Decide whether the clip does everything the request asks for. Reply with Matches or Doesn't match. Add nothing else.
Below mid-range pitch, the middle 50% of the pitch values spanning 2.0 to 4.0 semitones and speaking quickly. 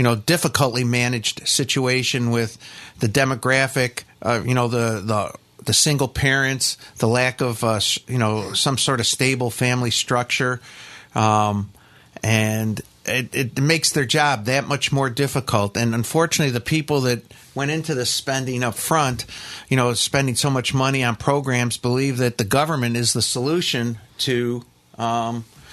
Doesn't match